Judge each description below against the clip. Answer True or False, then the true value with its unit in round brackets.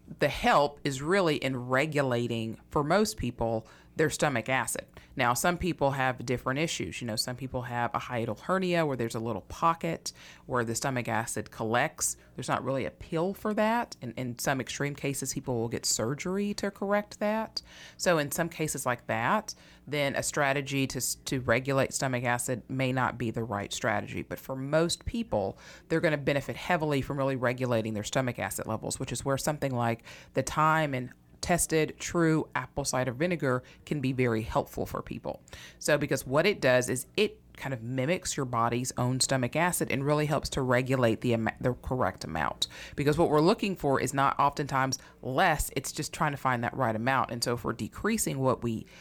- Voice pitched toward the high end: False (135 Hz)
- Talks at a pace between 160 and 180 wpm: False (195 wpm)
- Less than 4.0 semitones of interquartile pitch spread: False (4.3 semitones)